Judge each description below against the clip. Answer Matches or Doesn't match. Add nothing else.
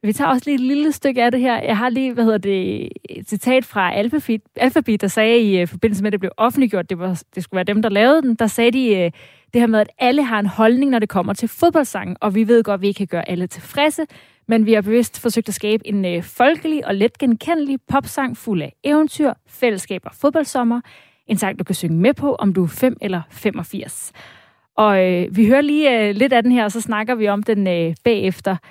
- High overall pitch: Matches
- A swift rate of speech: Matches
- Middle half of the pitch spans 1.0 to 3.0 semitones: Doesn't match